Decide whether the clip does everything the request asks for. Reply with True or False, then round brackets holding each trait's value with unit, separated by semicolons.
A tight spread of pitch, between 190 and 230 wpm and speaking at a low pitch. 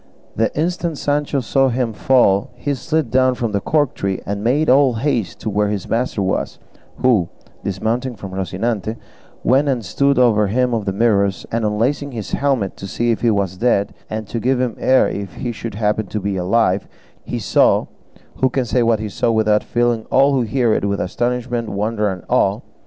False (3.9 semitones; 195 wpm; 115 Hz)